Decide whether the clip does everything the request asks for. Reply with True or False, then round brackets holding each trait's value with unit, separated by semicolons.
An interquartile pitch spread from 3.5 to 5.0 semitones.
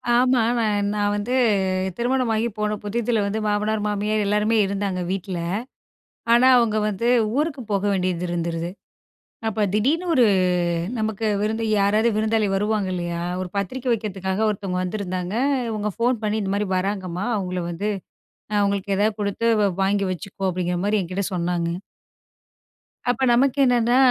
False (2.7 semitones)